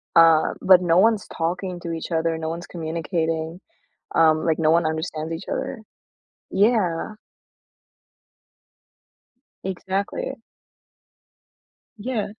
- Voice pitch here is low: No, medium, 170 Hz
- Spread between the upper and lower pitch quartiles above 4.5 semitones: No, average, 2.8 semitones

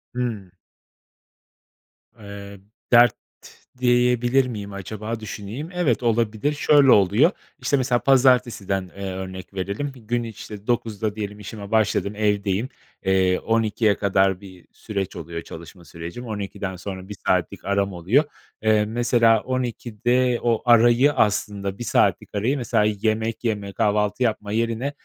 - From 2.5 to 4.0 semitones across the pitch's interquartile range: Yes, average, 3.3 semitones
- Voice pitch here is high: No, low, 110 Hz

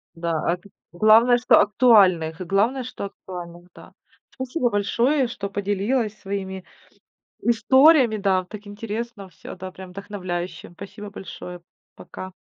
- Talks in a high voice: Yes, high, 200 Hz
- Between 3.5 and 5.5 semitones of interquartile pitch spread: Yes, average, 3.9 semitones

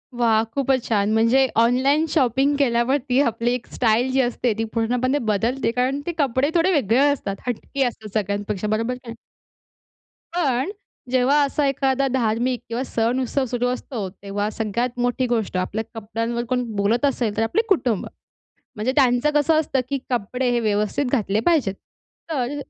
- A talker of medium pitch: No, high, 245 Hz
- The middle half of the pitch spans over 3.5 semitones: No, average, 3.2 semitones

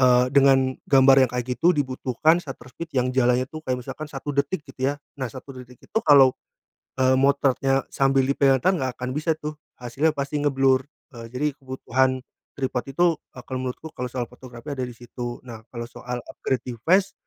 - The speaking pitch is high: No, low, 130 Hz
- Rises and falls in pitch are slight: Yes, narrow, 2.1 semitones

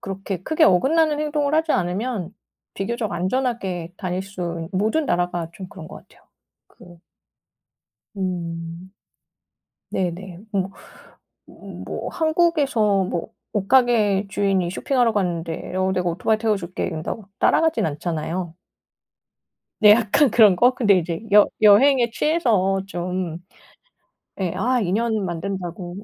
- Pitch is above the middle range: Yes, high, 195 Hz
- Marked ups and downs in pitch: No, average, 4.9 semitones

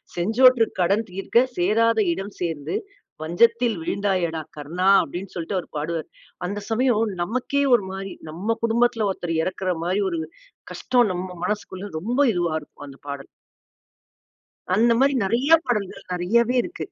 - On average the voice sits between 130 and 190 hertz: No, high, 200 Hz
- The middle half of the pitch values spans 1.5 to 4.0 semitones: No, average, 4.8 semitones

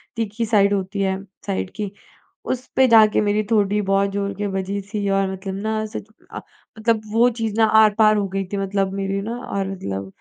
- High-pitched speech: Yes, high, 200 Hz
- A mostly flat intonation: Yes, narrow, 1.9 semitones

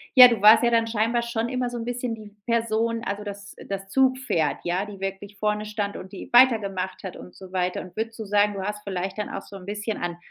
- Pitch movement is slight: No, average, 3.0 semitones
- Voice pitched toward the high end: Yes, high, 210 Hz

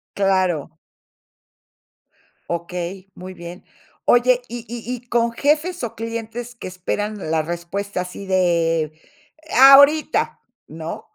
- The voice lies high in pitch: Yes, high, 200 Hz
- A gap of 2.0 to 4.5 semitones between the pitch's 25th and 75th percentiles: No, wide, 5.6 semitones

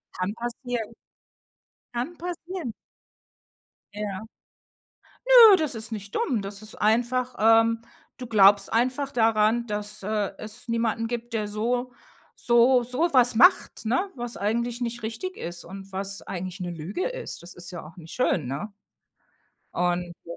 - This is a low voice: No, high, 225 Hz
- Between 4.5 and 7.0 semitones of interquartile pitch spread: No, average, 3.6 semitones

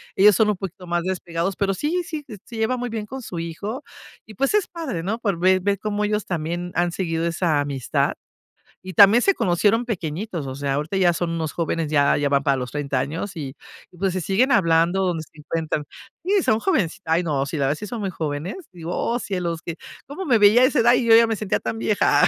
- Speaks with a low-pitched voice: No, medium, 185 Hz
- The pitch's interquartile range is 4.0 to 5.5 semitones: Yes, average, 5.0 semitones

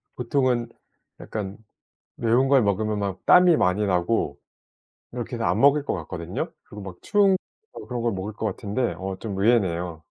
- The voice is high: No, low, 110 Hz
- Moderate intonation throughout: Yes, average, 4.4 semitones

